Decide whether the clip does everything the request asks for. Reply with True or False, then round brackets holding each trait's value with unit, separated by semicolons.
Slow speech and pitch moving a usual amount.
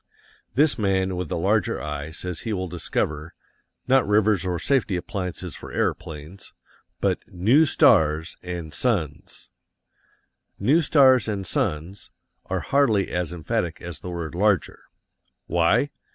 True (130 wpm; 4.5 semitones)